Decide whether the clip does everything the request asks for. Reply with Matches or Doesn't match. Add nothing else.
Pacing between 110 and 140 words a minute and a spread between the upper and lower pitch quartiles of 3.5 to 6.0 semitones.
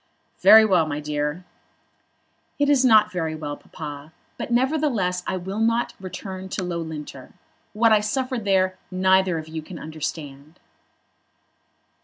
Matches